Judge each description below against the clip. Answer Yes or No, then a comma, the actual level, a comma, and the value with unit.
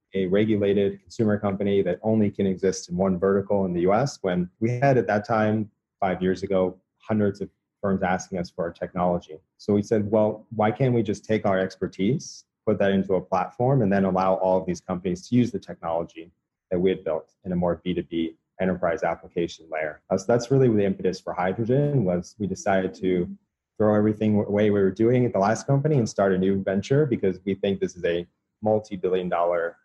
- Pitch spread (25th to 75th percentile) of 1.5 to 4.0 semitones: Yes, narrow, 2.5 semitones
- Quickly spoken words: Yes, fast, 215 wpm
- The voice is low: Yes, low, 100 Hz